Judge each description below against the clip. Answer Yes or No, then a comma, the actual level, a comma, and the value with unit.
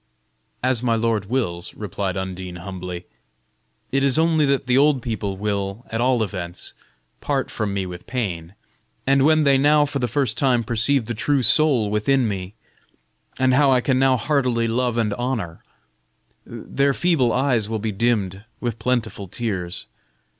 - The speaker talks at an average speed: Yes, average, 160 wpm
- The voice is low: Yes, low, 115 Hz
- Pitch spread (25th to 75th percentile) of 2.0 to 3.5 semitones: No, average, 4.9 semitones